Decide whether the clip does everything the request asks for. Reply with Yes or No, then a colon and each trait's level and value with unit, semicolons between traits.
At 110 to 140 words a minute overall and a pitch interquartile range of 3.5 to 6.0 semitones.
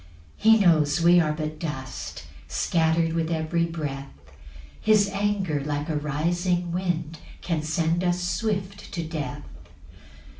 No: slow, 135 wpm; narrow, 2.6 semitones